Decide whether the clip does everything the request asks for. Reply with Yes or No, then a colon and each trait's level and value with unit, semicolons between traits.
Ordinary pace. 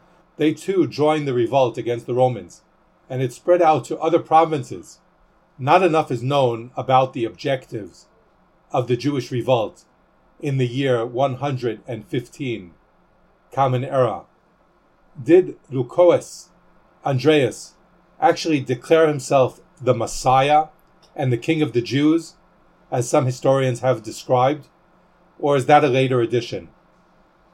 No: slow, 125 wpm